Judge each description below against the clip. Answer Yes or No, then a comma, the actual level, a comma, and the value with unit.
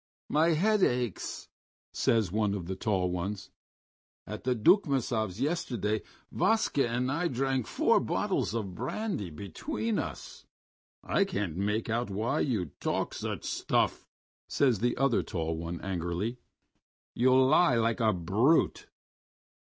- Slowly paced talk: Yes, slow, 130 wpm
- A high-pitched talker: No, low, 115 Hz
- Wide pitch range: Yes, wide, 5.7 semitones